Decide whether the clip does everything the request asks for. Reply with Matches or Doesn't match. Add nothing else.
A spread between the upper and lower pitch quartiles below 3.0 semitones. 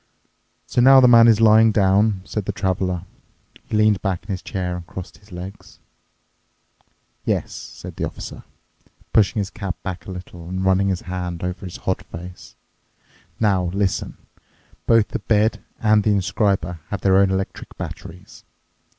Matches